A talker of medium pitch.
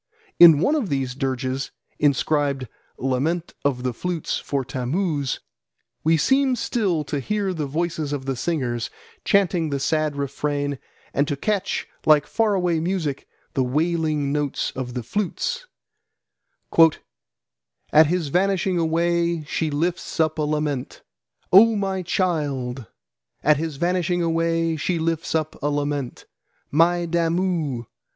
Yes: medium, 155 Hz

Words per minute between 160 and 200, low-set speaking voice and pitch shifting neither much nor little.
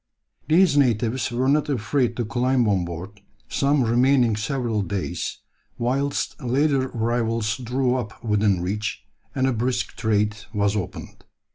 No: slow, 135 wpm; low, 120 Hz; average, 3.8 semitones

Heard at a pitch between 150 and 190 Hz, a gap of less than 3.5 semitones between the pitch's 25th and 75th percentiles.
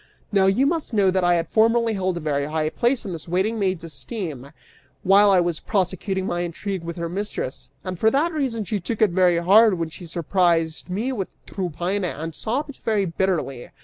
No: medium, 185 Hz; average, 4.1 semitones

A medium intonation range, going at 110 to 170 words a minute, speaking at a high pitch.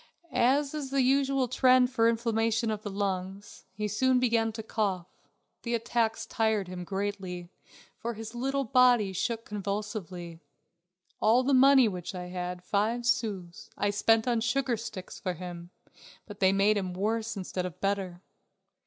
Yes: average, 4.0 semitones; average, 155 wpm; high, 215 Hz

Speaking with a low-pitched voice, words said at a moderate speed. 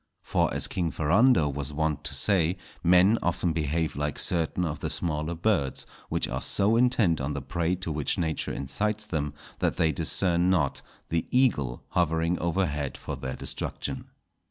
Yes: very low, 80 Hz; average, 165 wpm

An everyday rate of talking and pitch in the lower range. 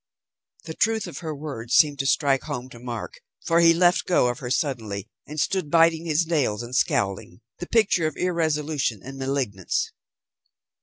No: average, 170 wpm; medium, 145 Hz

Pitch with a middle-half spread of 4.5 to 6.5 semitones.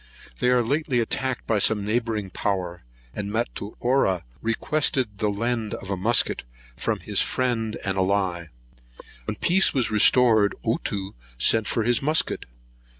No: average, 3.5 semitones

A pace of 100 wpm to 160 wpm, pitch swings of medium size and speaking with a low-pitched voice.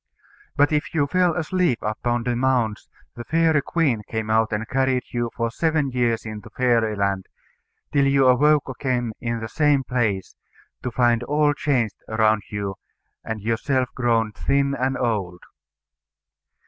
Yes: average, 150 wpm; average, 3.9 semitones; low, 120 Hz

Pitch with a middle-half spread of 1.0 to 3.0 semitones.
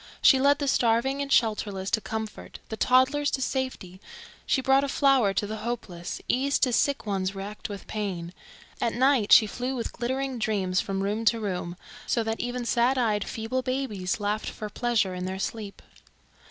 No: average, 4.3 semitones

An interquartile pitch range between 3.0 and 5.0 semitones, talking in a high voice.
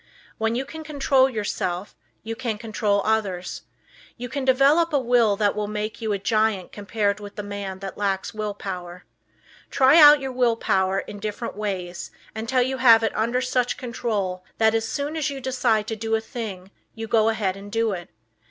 Yes: average, 3.6 semitones; high, 220 Hz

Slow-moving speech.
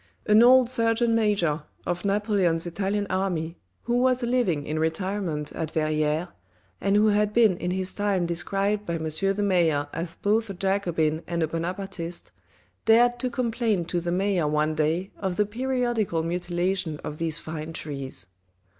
No: average, 160 wpm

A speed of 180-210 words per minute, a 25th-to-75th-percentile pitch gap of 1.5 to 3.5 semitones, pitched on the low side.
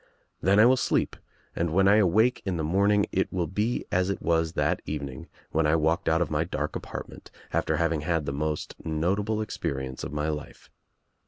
No: average, 195 wpm; average, 4.3 semitones; very low, 85 Hz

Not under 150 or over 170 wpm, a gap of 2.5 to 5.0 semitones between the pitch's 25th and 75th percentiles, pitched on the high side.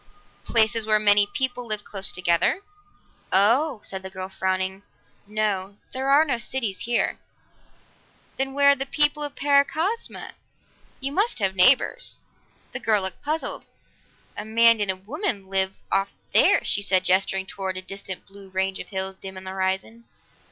No: average, 160 wpm; wide, 5.6 semitones; high, 205 Hz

